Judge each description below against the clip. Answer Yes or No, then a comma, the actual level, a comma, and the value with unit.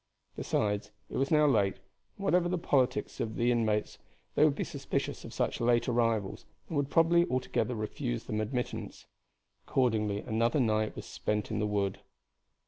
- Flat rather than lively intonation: No, average, 4.1 semitones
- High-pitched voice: No, low, 115 Hz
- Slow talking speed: No, average, 165 wpm